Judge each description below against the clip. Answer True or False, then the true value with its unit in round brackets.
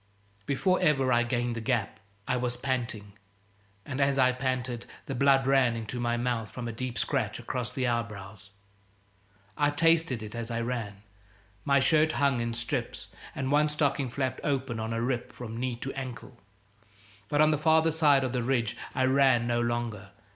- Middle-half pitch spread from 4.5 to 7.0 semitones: False (2.7 semitones)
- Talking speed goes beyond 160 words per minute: True (180 wpm)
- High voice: False (125 Hz)